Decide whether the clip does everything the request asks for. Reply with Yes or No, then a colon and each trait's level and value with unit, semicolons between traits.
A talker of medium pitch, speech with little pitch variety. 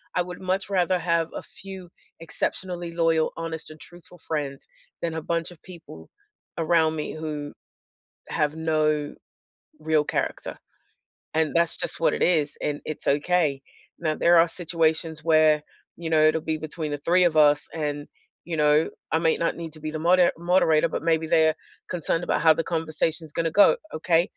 Yes: medium, 160 Hz; narrow, 1.6 semitones